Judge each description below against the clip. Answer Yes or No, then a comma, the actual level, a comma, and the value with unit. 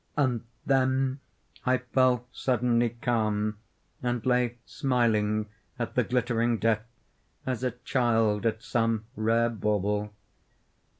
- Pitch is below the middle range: Yes, low, 120 Hz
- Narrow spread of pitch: Yes, narrow, 2.3 semitones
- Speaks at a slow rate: Yes, slow, 110 wpm